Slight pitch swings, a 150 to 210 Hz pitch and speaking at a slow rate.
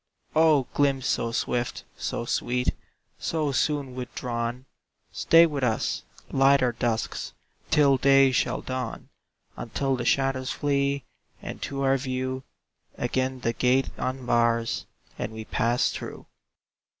No: narrow, 2.2 semitones; low, 130 Hz; slow, 125 wpm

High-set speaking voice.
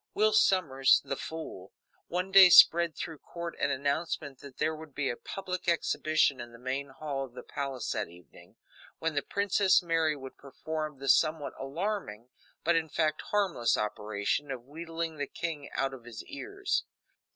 No: medium, 155 Hz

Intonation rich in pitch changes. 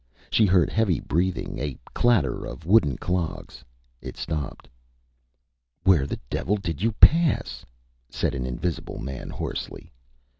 Yes: wide, 6.2 semitones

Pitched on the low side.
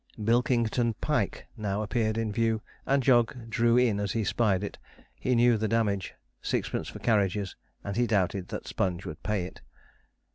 Yes: low, 110 Hz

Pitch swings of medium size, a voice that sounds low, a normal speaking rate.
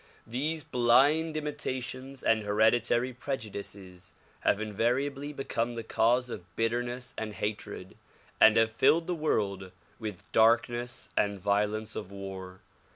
No: average, 3.8 semitones; low, 115 Hz; slow, 120 wpm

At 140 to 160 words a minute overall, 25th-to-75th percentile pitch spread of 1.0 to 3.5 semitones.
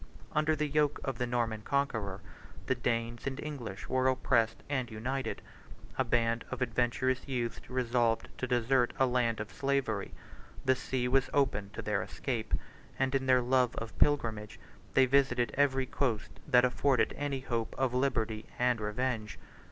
Yes: average, 155 wpm; narrow, 2.5 semitones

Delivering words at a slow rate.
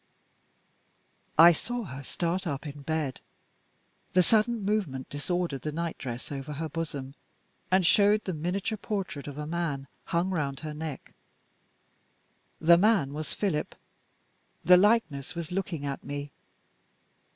Yes: slow, 130 wpm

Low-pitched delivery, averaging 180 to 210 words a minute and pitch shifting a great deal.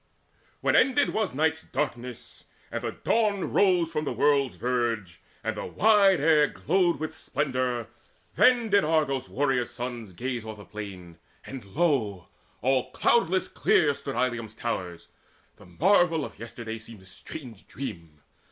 No: low, 130 Hz; average, 145 wpm; wide, 6.3 semitones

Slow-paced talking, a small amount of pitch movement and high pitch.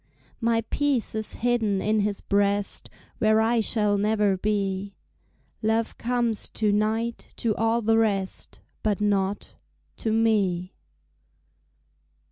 Yes: slow, 115 wpm; narrow, 1.9 semitones; high, 215 Hz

